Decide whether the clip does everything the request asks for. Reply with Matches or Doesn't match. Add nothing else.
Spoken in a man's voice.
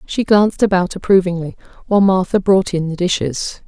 Doesn't match